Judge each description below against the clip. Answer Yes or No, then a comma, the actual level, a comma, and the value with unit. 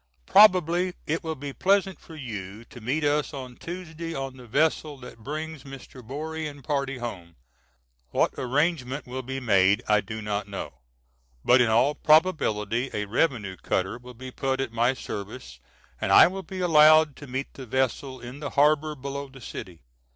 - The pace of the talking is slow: No, average, 175 wpm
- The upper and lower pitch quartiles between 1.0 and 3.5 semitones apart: No, average, 4.4 semitones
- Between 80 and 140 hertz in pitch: Yes, low, 135 Hz